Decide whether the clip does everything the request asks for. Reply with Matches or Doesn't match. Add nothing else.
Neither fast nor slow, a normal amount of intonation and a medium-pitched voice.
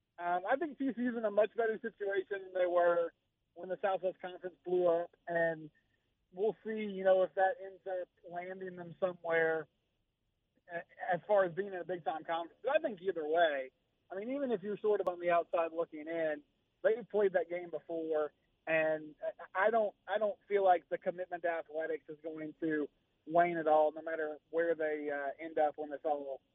Matches